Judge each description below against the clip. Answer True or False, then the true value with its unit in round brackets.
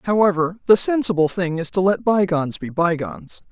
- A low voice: False (180 Hz)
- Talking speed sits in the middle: True (170 wpm)